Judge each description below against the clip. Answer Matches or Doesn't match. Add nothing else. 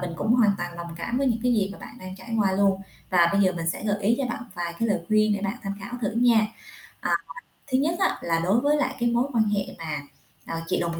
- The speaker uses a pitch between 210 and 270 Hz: Doesn't match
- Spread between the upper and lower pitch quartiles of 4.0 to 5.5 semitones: Matches